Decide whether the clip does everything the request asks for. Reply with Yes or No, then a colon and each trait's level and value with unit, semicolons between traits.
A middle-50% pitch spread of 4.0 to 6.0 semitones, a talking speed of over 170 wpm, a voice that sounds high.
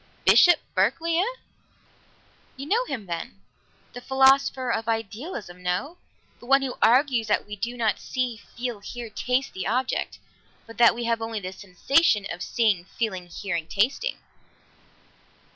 No: average, 4.7 semitones; average, 145 wpm; high, 235 Hz